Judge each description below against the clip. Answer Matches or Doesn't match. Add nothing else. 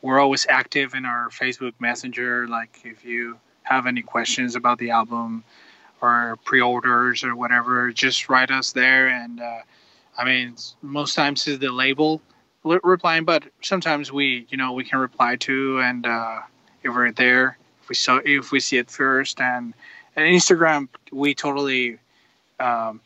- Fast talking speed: Doesn't match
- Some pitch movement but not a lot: Doesn't match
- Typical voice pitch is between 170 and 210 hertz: Doesn't match